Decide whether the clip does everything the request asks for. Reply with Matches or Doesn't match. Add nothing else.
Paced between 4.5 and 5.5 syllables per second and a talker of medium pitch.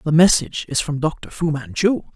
Matches